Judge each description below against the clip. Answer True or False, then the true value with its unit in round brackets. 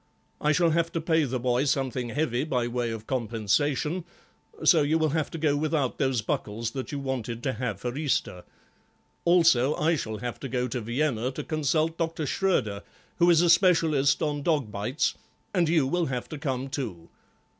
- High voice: False (140 Hz)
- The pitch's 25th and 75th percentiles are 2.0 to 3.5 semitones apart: False (4.6 semitones)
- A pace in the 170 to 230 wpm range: True (190 wpm)